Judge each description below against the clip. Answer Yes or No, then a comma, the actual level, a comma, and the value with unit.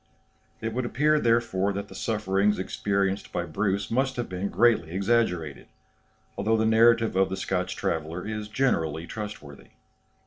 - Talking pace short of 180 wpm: Yes, average, 145 wpm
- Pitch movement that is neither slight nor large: Yes, average, 3.5 semitones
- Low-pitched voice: Yes, low, 100 Hz